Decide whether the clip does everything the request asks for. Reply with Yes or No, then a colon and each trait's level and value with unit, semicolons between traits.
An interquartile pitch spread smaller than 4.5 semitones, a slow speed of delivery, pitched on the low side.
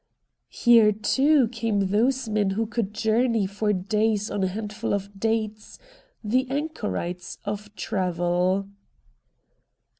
No: narrow, 2.4 semitones; slow, 115 wpm; high, 210 Hz